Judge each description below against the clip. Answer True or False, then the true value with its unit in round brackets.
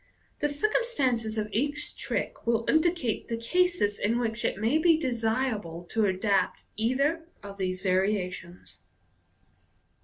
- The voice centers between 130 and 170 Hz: False (230 Hz)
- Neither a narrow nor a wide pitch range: False (6.2 semitones)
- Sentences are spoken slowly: True (125 wpm)